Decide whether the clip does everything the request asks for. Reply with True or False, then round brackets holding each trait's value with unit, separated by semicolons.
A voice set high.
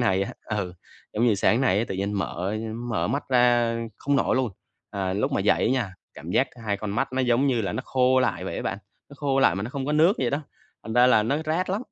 False (120 Hz)